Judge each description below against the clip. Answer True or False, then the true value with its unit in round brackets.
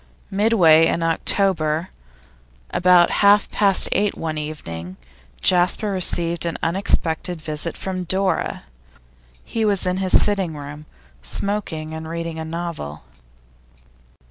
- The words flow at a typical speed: False (115 wpm)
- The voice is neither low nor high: True (170 Hz)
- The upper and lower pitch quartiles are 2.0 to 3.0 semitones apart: False (3.4 semitones)